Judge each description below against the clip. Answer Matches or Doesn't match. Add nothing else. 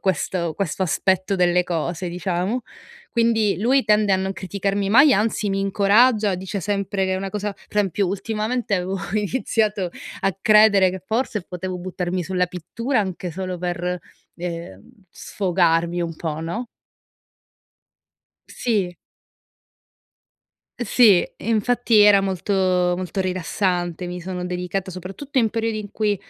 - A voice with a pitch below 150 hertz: Doesn't match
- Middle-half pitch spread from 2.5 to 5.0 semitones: Matches